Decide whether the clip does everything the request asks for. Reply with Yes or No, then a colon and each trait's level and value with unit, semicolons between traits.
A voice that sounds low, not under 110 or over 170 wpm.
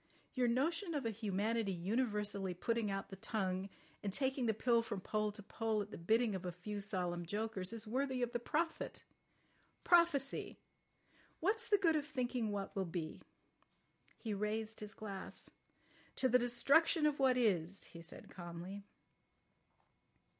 No: high, 220 Hz; average, 160 wpm